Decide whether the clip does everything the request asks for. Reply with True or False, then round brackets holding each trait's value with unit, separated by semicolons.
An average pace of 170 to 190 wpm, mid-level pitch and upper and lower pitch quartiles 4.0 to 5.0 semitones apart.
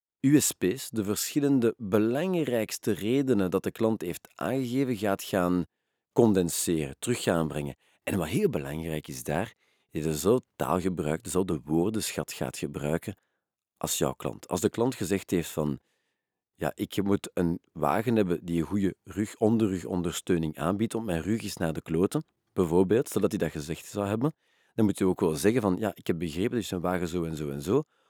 False (185 wpm; 95 Hz; 4.7 semitones)